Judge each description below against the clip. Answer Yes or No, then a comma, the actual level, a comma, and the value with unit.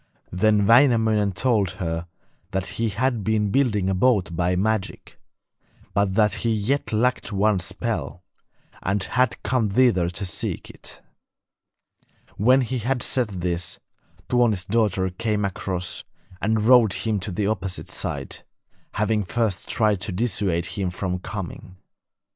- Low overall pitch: Yes, low, 105 Hz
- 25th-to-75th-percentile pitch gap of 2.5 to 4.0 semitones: Yes, average, 3.5 semitones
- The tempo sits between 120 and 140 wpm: Yes, slow, 135 wpm